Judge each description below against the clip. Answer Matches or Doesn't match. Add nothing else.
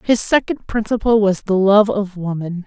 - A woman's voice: Matches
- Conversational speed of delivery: Matches